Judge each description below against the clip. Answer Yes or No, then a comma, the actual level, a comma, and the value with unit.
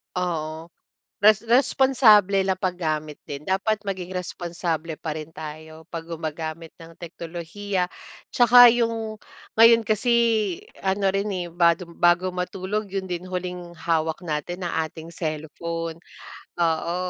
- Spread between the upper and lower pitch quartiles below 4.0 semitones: Yes, average, 3.3 semitones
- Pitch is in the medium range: Yes, medium, 175 Hz